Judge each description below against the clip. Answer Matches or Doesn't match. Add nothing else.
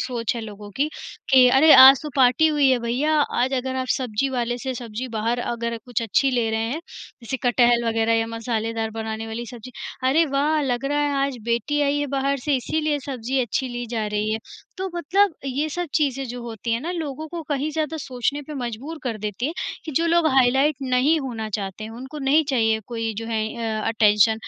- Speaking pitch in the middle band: Doesn't match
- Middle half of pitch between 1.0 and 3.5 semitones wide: Doesn't match